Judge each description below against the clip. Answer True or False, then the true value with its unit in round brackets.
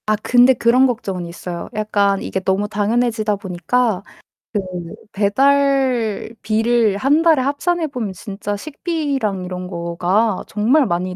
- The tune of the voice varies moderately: True (4.9 semitones)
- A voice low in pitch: False (215 Hz)